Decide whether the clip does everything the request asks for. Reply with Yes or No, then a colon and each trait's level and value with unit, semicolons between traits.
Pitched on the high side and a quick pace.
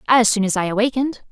Yes: high, 225 Hz; fast, 230 wpm